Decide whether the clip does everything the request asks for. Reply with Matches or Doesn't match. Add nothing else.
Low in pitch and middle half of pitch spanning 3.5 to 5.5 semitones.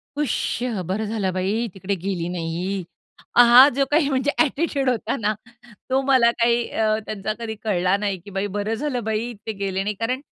Doesn't match